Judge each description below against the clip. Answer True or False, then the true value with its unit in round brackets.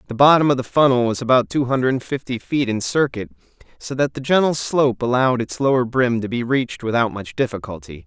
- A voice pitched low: True (125 Hz)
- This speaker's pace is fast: True (210 wpm)